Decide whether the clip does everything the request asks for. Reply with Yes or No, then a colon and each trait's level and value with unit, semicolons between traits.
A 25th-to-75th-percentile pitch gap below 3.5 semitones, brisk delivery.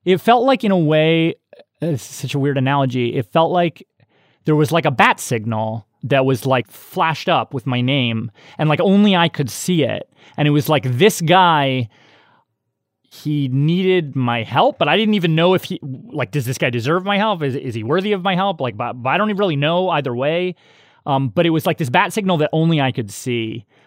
No: average, 5.3 semitones; fast, 225 wpm